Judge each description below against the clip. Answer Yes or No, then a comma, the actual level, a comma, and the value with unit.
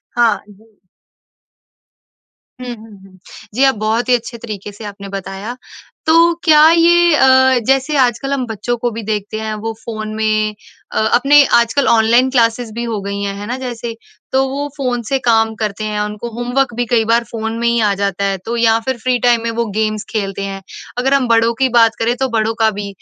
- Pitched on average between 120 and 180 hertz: No, high, 230 Hz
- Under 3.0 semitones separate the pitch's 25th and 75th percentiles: Yes, narrow, 2.6 semitones